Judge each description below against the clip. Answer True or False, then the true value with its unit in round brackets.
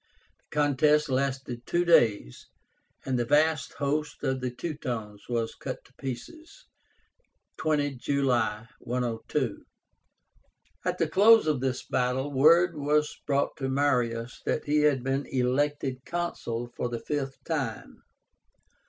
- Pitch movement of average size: True (3.3 semitones)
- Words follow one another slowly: True (125 wpm)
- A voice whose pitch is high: False (135 Hz)